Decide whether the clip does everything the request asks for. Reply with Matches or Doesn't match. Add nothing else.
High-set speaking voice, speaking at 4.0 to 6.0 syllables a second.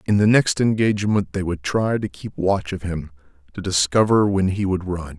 Doesn't match